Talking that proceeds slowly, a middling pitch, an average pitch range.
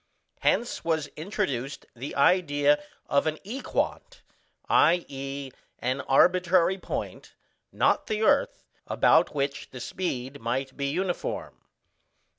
Yes: slow, 105 wpm; medium, 145 Hz; average, 4.9 semitones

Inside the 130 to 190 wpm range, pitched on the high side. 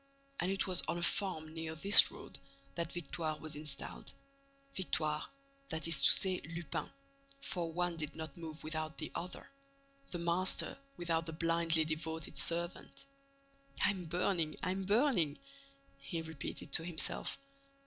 No: average, 140 wpm; medium, 165 Hz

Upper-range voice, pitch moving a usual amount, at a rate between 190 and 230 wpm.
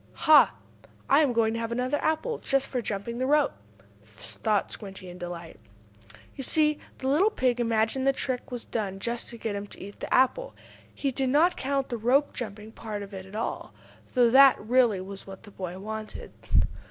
Yes: high, 235 Hz; average, 4.8 semitones; average, 195 wpm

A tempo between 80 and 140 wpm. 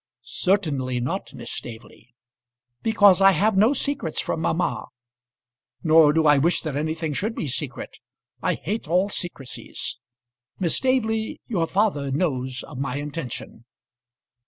Yes: slow, 135 wpm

